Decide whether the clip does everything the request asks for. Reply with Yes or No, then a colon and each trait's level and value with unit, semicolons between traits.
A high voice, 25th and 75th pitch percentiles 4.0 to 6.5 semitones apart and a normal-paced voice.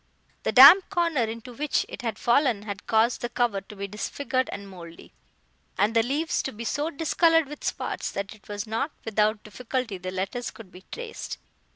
Yes: high, 230 Hz; average, 5.2 semitones; average, 190 wpm